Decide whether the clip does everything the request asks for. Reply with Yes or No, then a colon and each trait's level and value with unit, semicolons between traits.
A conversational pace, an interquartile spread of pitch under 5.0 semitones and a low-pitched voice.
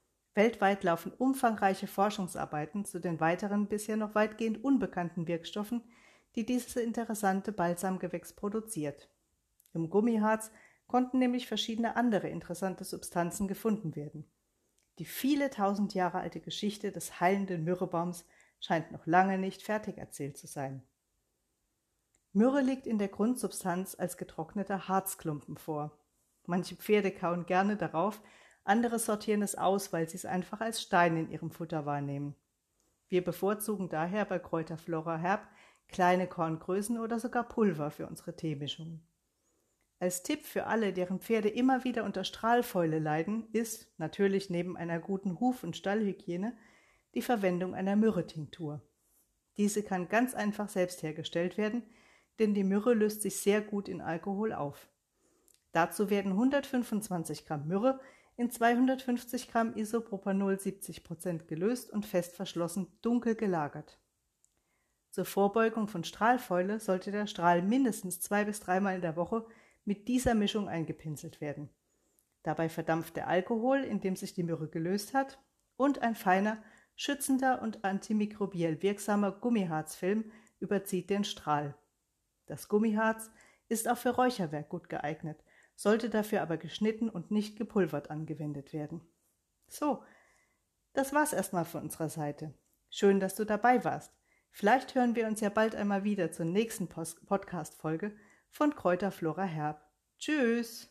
No: average, 135 wpm; average, 4.5 semitones; high, 195 Hz